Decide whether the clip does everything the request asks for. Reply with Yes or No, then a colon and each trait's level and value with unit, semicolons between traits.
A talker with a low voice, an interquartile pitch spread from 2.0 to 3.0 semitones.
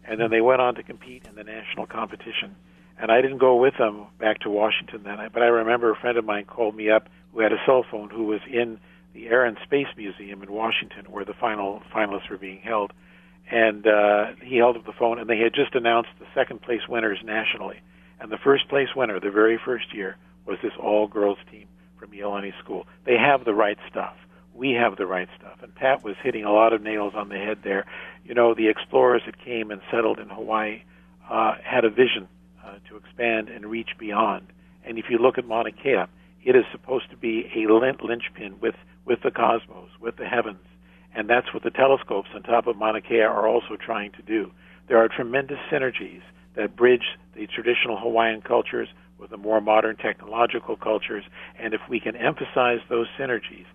Yes: low, 110 Hz; average, 2.7 semitones